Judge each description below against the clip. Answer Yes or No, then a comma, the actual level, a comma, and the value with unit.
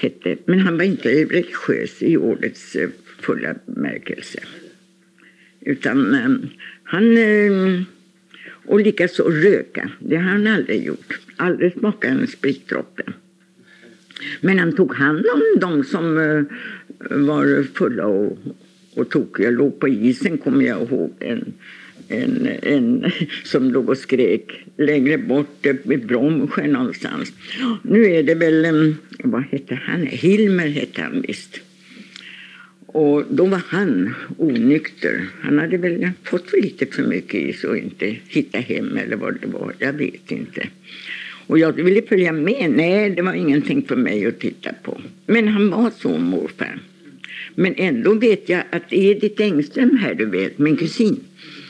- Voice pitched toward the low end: No, medium, 185 Hz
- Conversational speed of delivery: Yes, average, 140 wpm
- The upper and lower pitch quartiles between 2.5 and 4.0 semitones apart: No, wide, 5.5 semitones